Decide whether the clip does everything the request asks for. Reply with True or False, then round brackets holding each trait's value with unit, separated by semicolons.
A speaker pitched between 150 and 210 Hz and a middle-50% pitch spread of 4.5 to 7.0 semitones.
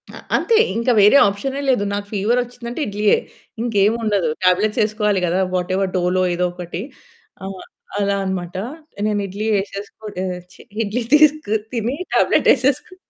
False (205 Hz; 3.7 semitones)